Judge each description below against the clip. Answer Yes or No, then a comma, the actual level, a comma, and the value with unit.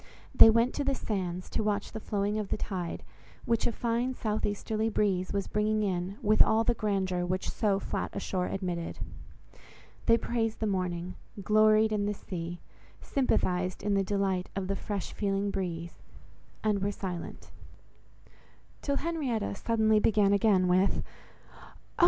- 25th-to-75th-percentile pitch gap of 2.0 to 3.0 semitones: Yes, average, 2.7 semitones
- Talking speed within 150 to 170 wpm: Yes, average, 155 wpm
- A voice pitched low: No, high, 205 Hz